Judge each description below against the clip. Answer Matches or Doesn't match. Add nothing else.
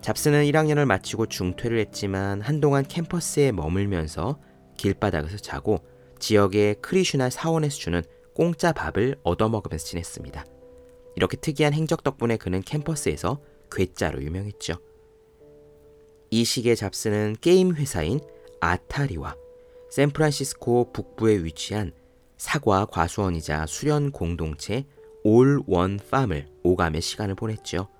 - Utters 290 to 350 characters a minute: Matches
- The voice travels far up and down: Matches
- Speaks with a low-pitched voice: Matches